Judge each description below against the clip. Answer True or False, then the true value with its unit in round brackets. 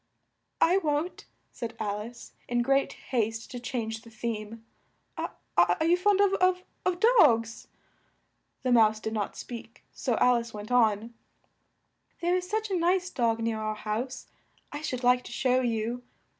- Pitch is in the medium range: False (240 Hz)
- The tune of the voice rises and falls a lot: True (5.9 semitones)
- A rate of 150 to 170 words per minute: True (155 wpm)